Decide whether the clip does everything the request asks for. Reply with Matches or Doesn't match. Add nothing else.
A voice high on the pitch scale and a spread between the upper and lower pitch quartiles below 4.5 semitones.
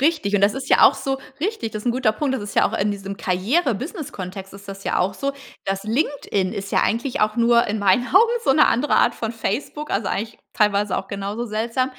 Doesn't match